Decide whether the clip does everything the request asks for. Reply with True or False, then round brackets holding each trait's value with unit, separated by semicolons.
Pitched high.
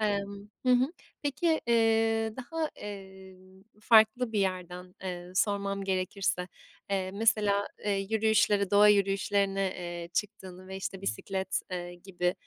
True (200 Hz)